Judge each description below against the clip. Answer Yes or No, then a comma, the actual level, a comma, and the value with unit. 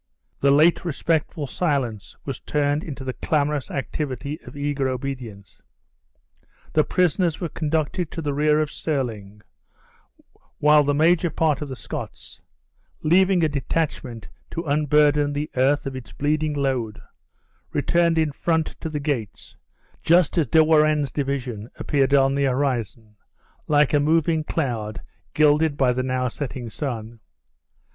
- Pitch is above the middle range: No, medium, 145 Hz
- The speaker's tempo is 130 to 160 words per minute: Yes, average, 140 wpm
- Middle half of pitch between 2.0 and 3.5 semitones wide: Yes, average, 2.9 semitones